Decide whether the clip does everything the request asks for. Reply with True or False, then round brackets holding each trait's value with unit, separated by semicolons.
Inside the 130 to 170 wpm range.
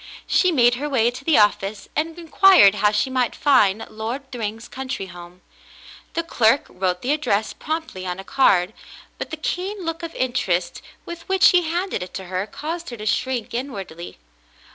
False (185 wpm)